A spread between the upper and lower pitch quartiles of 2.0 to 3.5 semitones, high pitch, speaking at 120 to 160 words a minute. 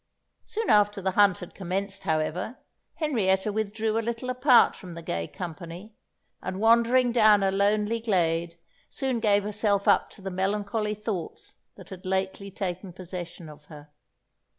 Yes: average, 3.1 semitones; high, 200 Hz; average, 150 wpm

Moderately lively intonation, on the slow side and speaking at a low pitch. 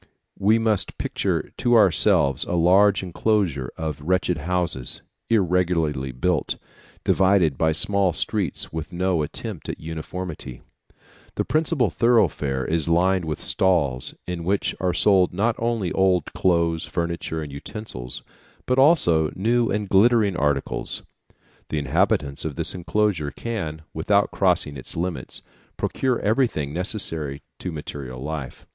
Yes: average, 4.6 semitones; slow, 130 wpm; very low, 90 Hz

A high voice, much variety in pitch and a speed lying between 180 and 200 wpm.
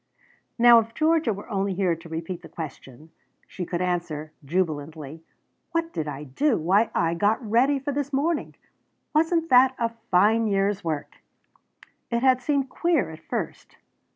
No: high, 200 Hz; wide, 8.1 semitones; average, 155 wpm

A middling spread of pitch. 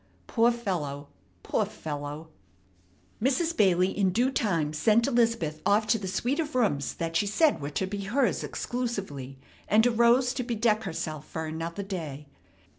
No: wide, 6.8 semitones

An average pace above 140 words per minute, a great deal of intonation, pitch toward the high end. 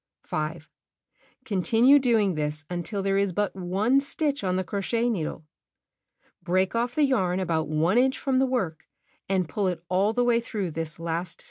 Yes: average, 175 wpm; wide, 5.7 semitones; high, 195 Hz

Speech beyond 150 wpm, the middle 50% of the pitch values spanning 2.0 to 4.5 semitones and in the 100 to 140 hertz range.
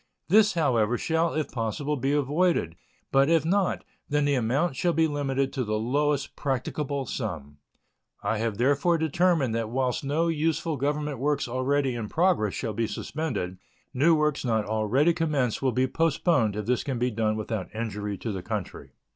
No: average, 170 wpm; average, 5.1 semitones; low, 135 Hz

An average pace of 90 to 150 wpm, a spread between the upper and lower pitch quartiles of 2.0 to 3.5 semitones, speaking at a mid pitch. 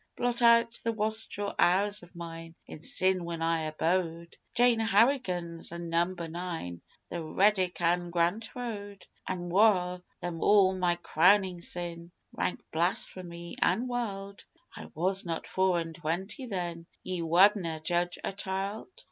Yes: average, 140 wpm; average, 3.1 semitones; medium, 180 Hz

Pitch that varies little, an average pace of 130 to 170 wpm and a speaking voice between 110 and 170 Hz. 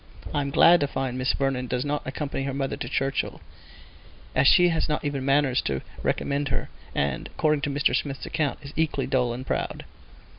No: narrow, 1.8 semitones; average, 195 wpm; medium, 140 Hz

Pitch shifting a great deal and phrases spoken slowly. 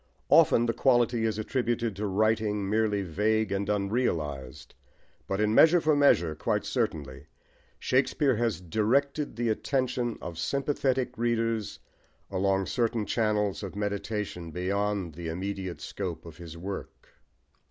No: average, 3.9 semitones; slow, 130 wpm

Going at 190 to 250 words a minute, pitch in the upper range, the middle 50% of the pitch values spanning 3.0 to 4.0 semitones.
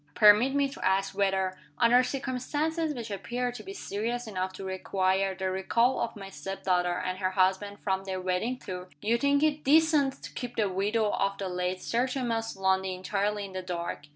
No: average, 195 wpm; high, 200 Hz; average, 4.7 semitones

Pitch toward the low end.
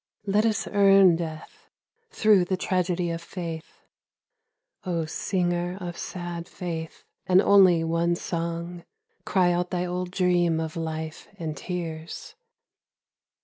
No: medium, 175 Hz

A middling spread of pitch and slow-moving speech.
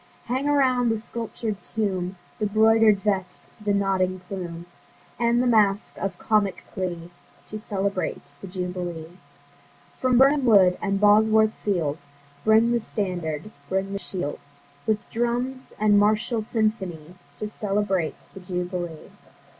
Yes: average, 3.3 semitones; slow, 130 wpm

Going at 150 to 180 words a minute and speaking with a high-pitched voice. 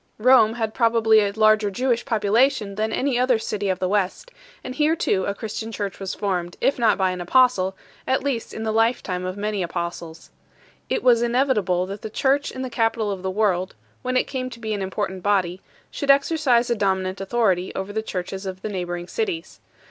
No: average, 200 wpm; high, 215 Hz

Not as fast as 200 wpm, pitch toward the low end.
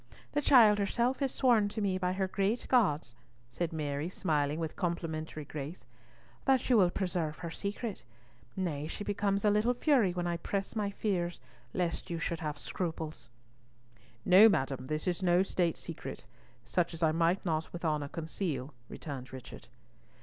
No: average, 165 wpm; medium, 175 Hz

